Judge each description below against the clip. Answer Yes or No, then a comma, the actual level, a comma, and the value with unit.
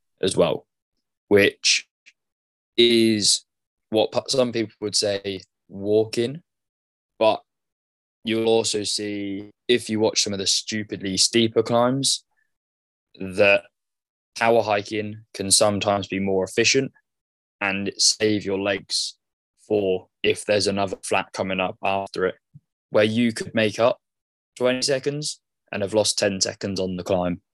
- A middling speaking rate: No, slow, 130 wpm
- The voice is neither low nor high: No, low, 105 Hz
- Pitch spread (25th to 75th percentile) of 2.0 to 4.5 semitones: Yes, average, 2.9 semitones